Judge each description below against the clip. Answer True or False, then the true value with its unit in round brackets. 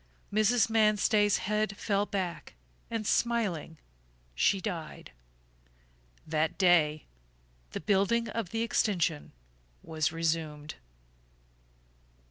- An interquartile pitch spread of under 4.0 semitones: False (4.9 semitones)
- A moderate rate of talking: False (90 wpm)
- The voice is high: True (195 Hz)